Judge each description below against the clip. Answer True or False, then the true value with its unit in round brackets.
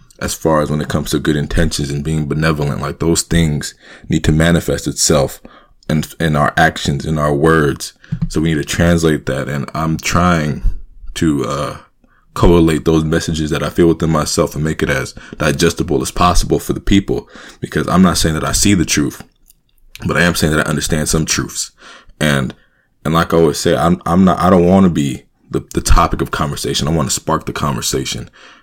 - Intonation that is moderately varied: False (2.2 semitones)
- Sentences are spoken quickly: True (210 wpm)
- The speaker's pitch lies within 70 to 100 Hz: True (80 Hz)